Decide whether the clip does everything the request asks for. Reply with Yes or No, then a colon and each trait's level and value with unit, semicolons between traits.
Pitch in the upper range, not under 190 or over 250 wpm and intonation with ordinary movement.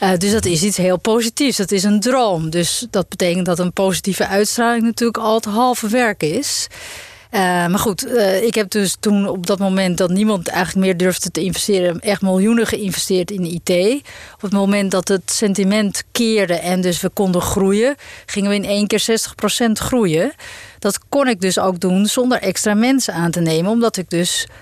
Yes: high, 200 Hz; average, 195 wpm; average, 3.2 semitones